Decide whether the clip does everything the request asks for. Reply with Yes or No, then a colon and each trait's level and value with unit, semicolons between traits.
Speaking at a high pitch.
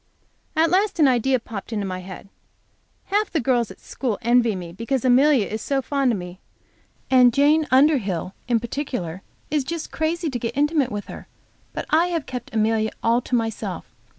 Yes: very high, 250 Hz